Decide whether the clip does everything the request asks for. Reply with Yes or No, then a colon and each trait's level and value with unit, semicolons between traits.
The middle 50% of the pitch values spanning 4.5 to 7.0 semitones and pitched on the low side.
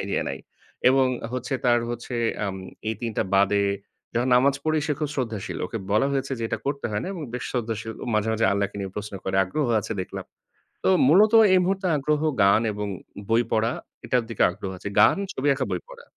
Yes: average, 4.8 semitones; low, 120 Hz